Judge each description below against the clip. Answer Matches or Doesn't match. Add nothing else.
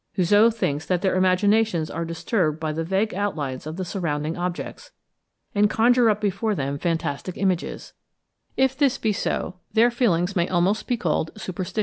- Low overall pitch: Doesn't match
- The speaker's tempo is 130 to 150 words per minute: Doesn't match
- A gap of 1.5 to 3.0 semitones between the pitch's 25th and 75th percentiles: Doesn't match